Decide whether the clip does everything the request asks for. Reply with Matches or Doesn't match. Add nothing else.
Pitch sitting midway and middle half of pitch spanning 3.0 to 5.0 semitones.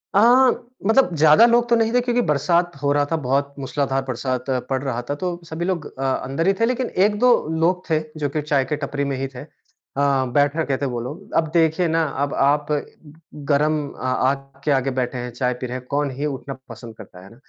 Matches